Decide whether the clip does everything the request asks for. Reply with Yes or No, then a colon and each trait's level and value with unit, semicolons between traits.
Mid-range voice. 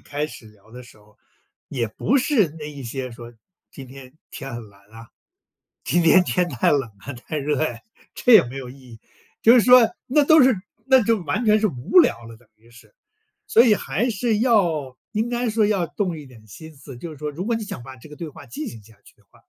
Yes: medium, 150 Hz